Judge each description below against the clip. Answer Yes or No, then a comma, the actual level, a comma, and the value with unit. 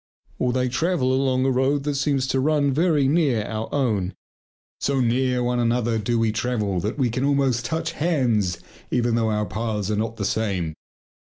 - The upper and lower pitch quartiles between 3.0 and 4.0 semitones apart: Yes, average, 3.6 semitones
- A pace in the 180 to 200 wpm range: Yes, average, 185 wpm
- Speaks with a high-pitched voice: No, low, 125 Hz